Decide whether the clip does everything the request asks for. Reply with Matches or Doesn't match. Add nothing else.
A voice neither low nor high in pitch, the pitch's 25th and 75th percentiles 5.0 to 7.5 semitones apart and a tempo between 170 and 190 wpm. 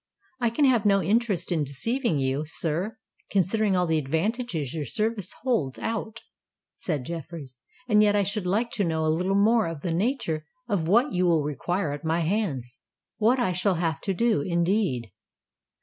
Matches